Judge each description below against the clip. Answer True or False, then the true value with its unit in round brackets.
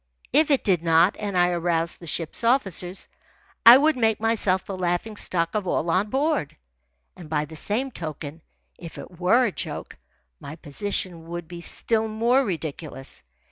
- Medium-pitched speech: True (180 Hz)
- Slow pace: False (170 wpm)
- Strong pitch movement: False (5.0 semitones)